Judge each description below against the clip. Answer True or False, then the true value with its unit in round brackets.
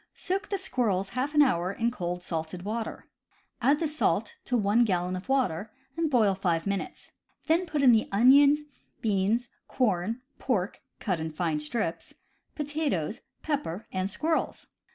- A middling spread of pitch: False (7.3 semitones)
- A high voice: True (220 Hz)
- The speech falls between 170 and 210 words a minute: False (155 wpm)